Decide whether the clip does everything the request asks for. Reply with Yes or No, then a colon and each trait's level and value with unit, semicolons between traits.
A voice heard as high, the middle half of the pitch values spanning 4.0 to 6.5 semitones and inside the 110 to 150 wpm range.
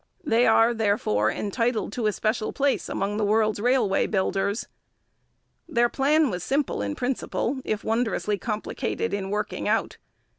No: high, 220 Hz; average, 3.2 semitones; average, 145 wpm